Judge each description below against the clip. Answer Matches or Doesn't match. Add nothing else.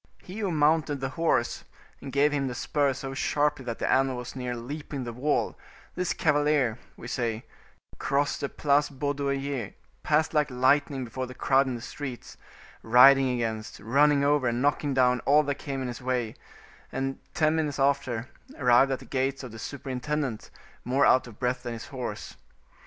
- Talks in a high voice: Doesn't match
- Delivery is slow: Doesn't match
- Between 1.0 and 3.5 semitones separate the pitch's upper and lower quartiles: Matches